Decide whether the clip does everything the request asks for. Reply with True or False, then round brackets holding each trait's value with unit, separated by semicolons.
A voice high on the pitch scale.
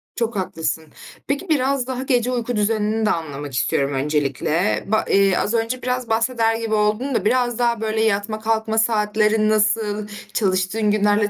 True (220 Hz)